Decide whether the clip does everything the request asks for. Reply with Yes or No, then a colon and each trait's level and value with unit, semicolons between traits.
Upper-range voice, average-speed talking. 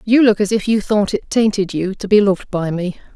No: high, 200 Hz; fast, 265 wpm